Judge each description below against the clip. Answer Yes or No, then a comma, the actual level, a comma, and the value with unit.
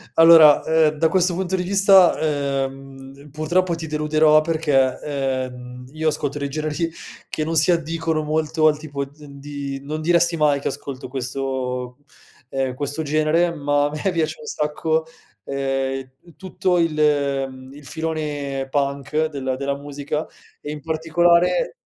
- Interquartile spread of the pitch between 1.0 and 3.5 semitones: Yes, average, 2.7 semitones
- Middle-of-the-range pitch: Yes, medium, 150 Hz